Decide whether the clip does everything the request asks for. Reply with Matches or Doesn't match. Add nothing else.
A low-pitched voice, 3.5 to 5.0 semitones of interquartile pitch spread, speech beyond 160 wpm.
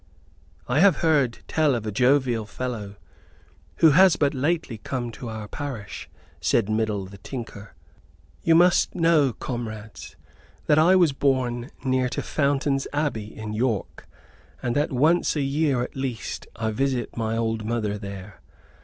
Doesn't match